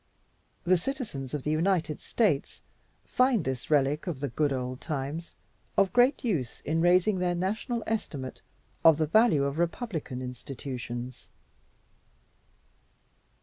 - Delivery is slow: Yes, slow, 125 wpm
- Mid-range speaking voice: Yes, medium, 155 Hz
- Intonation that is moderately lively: No, wide, 6.2 semitones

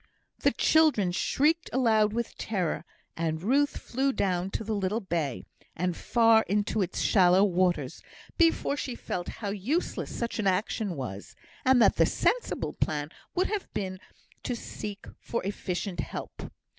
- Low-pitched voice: No, high, 205 Hz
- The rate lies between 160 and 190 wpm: No, average, 150 wpm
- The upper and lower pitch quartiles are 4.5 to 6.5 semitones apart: Yes, average, 4.9 semitones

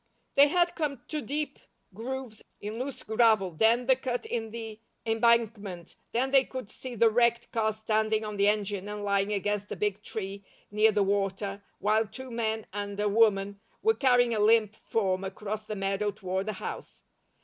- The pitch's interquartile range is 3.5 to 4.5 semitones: No, average, 2.7 semitones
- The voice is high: Yes, high, 215 Hz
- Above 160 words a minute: Yes, average, 180 wpm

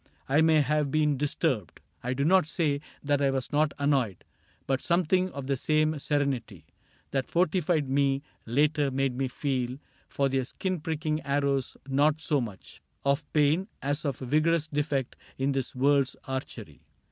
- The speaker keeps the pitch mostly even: Yes, narrow, 2.3 semitones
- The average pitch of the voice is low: No, medium, 145 Hz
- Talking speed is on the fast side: No, average, 160 wpm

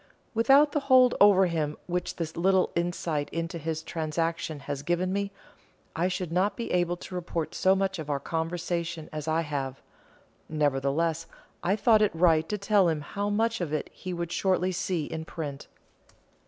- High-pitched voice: No, medium, 170 Hz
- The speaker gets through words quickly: No, average, 175 wpm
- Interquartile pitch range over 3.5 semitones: No, average, 3.2 semitones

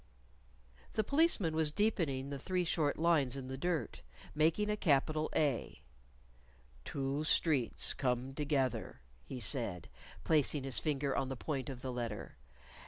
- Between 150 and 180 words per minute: No, average, 140 wpm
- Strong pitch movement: No, average, 3.4 semitones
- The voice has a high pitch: No, medium, 140 Hz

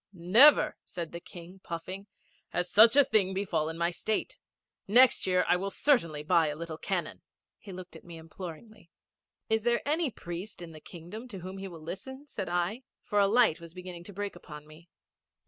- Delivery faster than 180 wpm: Yes, average, 190 wpm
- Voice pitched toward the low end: No, medium, 185 Hz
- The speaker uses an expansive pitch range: No, average, 4.1 semitones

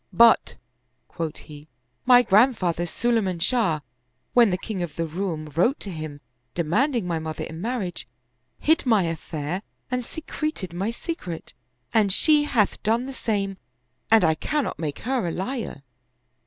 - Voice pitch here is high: Yes, high, 195 Hz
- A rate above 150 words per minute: Yes, average, 165 wpm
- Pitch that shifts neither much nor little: No, wide, 6.6 semitones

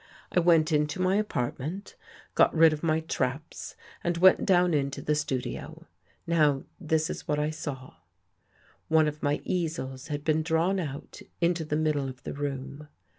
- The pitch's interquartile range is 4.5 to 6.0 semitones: No, narrow, 2.6 semitones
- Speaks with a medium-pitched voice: Yes, medium, 155 Hz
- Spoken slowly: No, average, 165 wpm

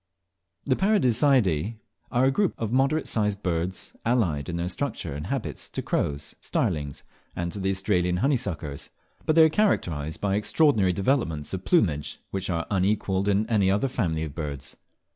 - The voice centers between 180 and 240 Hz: No, very low, 95 Hz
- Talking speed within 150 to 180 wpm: Yes, average, 160 wpm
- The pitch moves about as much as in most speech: No, wide, 6.9 semitones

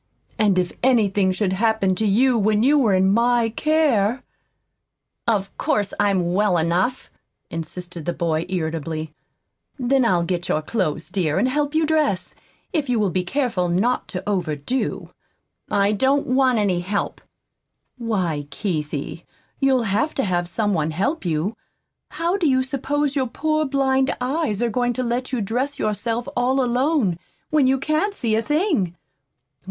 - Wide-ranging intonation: Yes, wide, 6.2 semitones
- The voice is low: No, high, 220 Hz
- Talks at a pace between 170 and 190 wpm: No, average, 160 wpm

